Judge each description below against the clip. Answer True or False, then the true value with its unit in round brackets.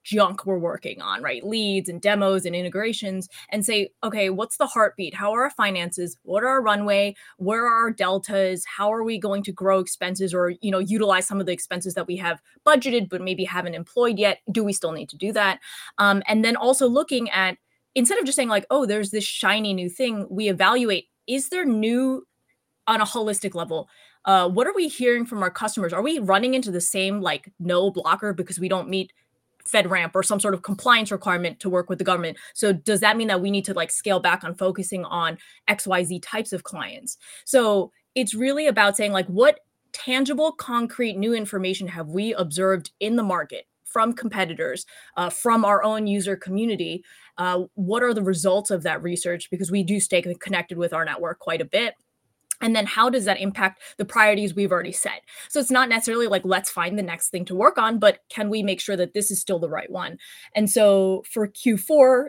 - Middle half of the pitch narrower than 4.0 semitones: True (3.4 semitones)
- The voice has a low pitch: False (200 Hz)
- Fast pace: True (215 wpm)